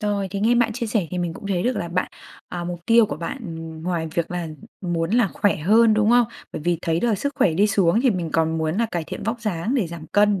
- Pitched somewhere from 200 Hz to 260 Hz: No, medium, 185 Hz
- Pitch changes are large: No, average, 4.6 semitones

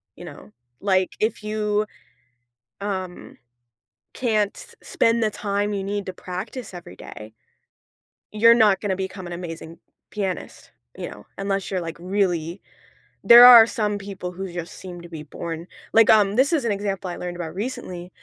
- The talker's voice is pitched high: Yes, high, 195 Hz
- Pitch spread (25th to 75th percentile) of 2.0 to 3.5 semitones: Yes, average, 3.0 semitones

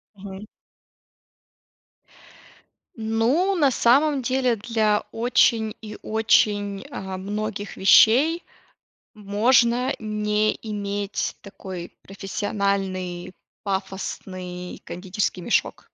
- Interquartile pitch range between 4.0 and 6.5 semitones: No, average, 2.9 semitones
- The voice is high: Yes, high, 210 Hz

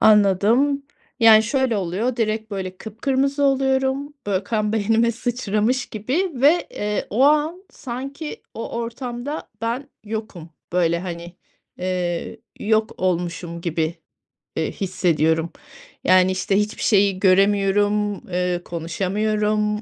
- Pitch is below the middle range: No, high, 210 Hz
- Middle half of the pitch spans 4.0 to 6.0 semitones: Yes, average, 4.7 semitones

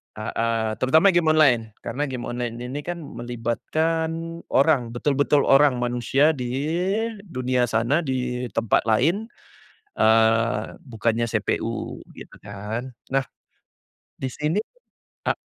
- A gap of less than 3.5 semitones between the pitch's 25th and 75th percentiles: No, average, 4.2 semitones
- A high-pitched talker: No, low, 125 Hz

